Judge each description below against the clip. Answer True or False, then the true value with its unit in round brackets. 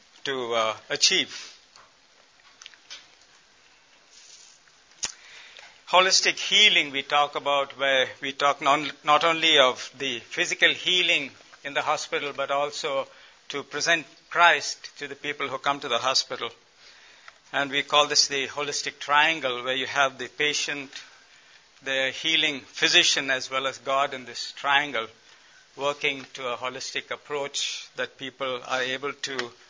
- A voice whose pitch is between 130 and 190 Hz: True (140 Hz)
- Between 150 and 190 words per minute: False (135 wpm)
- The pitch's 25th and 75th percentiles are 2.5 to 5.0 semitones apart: False (2.1 semitones)